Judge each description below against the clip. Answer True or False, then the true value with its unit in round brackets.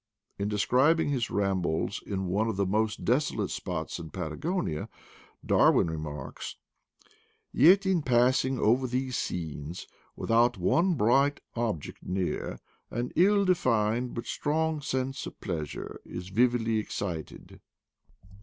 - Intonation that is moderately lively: False (6.0 semitones)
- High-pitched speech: False (115 Hz)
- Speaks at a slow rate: True (125 wpm)